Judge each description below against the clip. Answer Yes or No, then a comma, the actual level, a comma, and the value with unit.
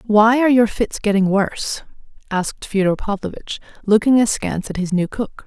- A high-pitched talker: Yes, high, 210 Hz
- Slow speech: No, average, 165 wpm